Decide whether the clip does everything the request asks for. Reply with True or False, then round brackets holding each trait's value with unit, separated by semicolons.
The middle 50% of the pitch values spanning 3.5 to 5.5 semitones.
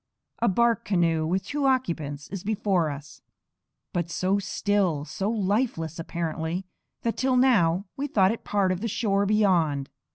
True (4.7 semitones)